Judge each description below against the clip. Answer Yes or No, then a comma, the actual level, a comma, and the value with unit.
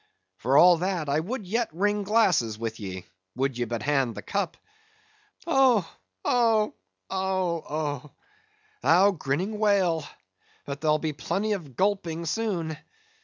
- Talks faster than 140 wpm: No, slow, 135 wpm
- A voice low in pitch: No, medium, 170 Hz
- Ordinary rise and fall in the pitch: No, wide, 5.9 semitones